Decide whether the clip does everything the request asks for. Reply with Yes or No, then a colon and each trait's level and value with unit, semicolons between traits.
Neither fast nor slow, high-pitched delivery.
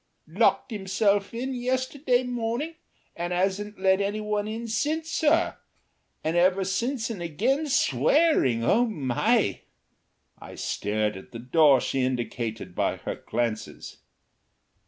No: slow, 120 wpm; high, 205 Hz